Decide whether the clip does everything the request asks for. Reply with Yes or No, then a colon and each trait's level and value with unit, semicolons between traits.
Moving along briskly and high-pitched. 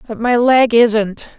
No: average, 175 wpm; high, 230 Hz